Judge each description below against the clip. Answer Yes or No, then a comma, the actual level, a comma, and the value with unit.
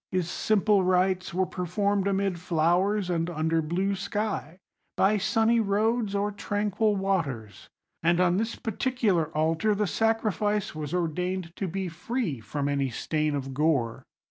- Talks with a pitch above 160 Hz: Yes, medium, 185 Hz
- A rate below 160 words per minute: Yes, average, 145 wpm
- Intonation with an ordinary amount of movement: Yes, average, 4.1 semitones